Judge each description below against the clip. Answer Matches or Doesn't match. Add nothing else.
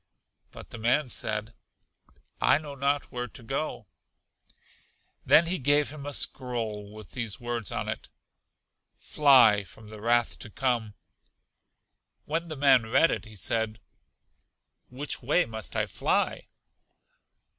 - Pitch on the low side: Matches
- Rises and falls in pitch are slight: Doesn't match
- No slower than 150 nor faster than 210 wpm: Doesn't match